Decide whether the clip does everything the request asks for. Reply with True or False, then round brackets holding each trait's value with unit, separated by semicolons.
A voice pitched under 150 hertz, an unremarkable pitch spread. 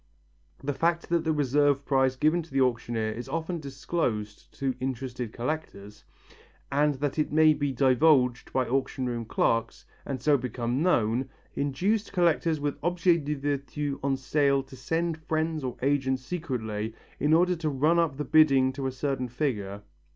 True (140 Hz; 3.6 semitones)